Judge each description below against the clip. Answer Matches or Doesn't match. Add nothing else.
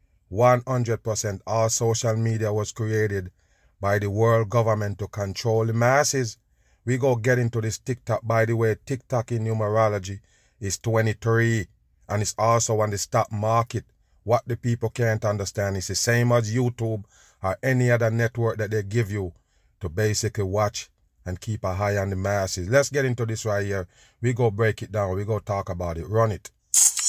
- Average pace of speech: Matches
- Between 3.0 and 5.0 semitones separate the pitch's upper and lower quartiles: Doesn't match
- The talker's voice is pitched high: Doesn't match